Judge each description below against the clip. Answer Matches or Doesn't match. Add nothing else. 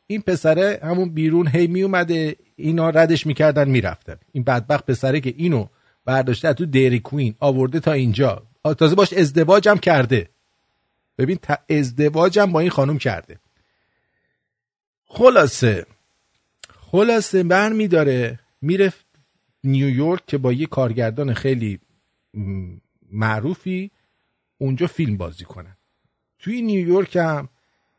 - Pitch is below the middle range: Doesn't match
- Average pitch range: Doesn't match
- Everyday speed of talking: Doesn't match